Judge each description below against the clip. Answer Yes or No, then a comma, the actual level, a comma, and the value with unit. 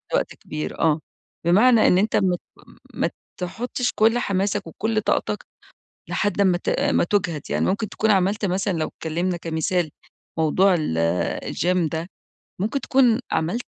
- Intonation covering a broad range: No, average, 4.1 semitones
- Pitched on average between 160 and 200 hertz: Yes, high, 190 Hz